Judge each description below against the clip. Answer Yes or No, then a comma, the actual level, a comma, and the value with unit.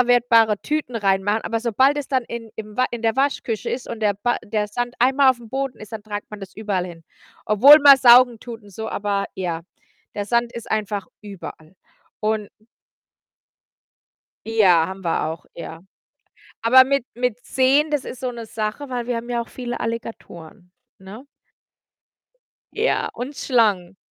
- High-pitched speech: Yes, high, 225 Hz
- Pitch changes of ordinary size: Yes, average, 3.4 semitones